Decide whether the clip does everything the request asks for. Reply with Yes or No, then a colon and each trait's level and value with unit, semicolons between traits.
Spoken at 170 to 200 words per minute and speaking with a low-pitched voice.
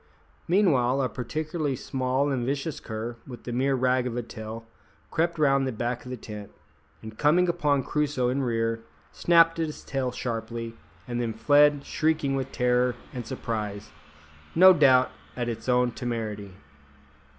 No: average, 160 wpm; low, 125 Hz